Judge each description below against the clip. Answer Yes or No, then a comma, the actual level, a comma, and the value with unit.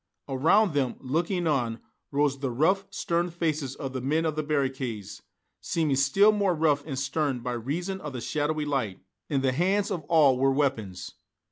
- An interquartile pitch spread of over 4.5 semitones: No, average, 3.8 semitones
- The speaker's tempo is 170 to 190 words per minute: Yes, average, 175 wpm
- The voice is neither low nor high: Yes, medium, 145 Hz